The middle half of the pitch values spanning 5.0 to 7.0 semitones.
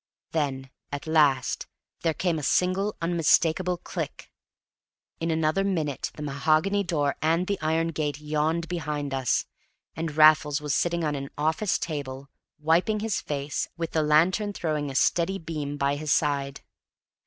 No: narrow, 2.6 semitones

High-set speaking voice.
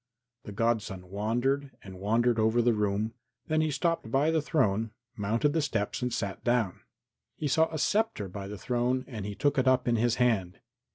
No: low, 120 Hz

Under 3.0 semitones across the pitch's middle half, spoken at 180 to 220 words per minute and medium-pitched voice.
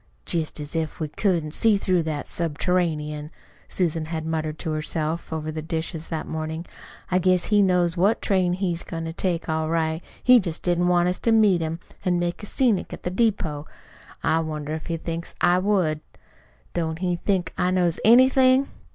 Yes: narrow, 2.6 semitones; average, 185 wpm; medium, 170 Hz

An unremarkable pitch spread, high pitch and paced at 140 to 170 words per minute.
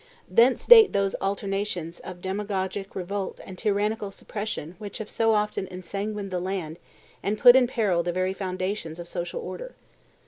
No: narrow, 2.3 semitones; high, 195 Hz; average, 160 wpm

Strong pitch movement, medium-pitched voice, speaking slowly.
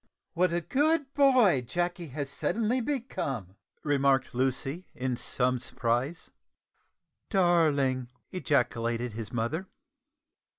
Yes: wide, 6.7 semitones; medium, 145 Hz; slow, 95 wpm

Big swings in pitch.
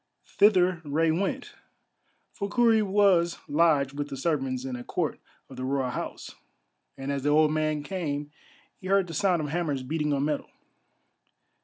No: average, 4.2 semitones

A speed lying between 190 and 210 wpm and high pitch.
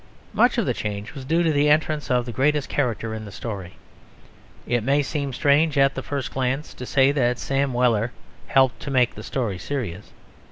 No: average, 200 wpm; low, 130 Hz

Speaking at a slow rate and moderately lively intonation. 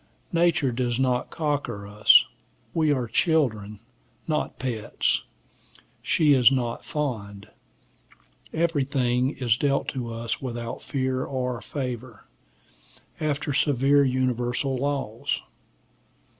Yes: slow, 100 wpm; average, 3.3 semitones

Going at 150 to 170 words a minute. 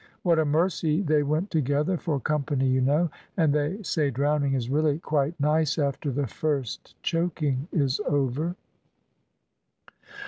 No: average, 140 wpm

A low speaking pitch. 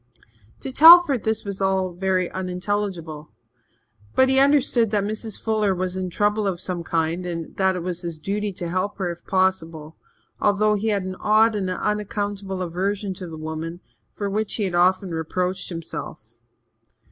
No: high, 190 Hz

